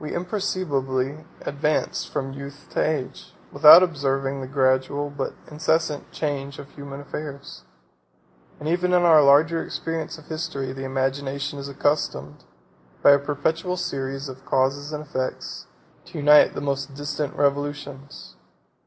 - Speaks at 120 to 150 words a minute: Yes, slow, 135 wpm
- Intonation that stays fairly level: Yes, narrow, 2.0 semitones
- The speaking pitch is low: No, medium, 145 Hz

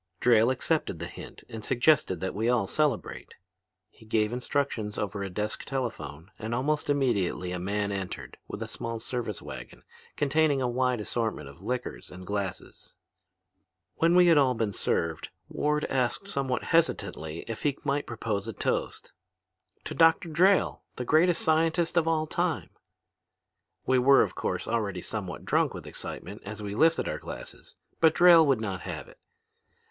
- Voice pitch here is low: Yes, low, 120 Hz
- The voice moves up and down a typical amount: No, wide, 6.5 semitones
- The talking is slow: No, average, 165 wpm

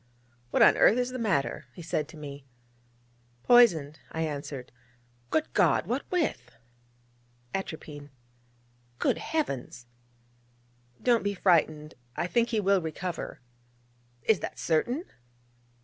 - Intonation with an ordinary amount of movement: No, wide, 7.5 semitones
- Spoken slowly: Yes, slow, 115 wpm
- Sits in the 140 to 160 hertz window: No, medium, 170 Hz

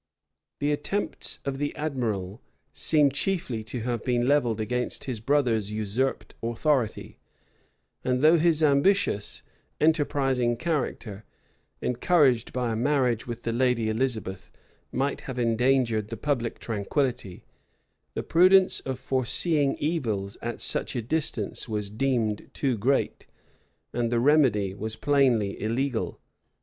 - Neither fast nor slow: No, slow, 125 wpm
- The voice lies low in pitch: Yes, low, 125 Hz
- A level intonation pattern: No, average, 4.3 semitones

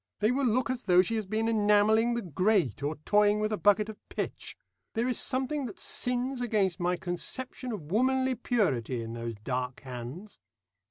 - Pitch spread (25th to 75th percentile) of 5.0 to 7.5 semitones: Yes, wide, 5.6 semitones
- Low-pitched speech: No, high, 210 Hz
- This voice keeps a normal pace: Yes, average, 180 wpm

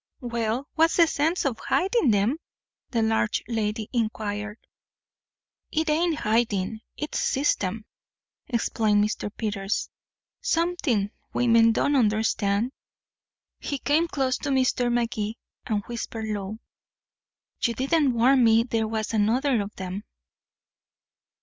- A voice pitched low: No, high, 230 Hz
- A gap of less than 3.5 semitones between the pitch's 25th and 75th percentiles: No, average, 4.0 semitones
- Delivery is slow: Yes, slow, 115 wpm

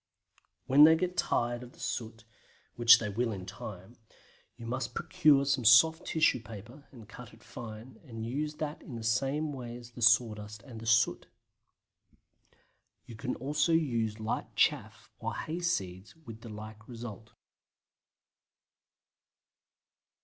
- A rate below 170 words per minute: Yes, average, 140 wpm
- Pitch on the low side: Yes, low, 120 Hz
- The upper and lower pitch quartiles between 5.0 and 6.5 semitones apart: No, average, 3.9 semitones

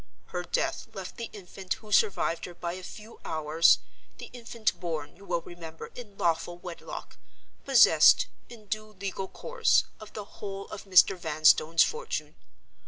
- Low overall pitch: No, high, 190 Hz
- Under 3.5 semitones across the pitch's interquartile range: No, average, 3.8 semitones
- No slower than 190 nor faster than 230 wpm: No, average, 155 wpm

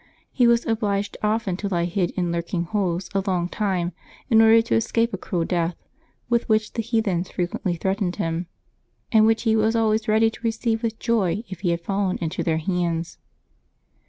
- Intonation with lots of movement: No, average, 4.2 semitones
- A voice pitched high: Yes, high, 200 Hz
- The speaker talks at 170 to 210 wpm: Yes, average, 190 wpm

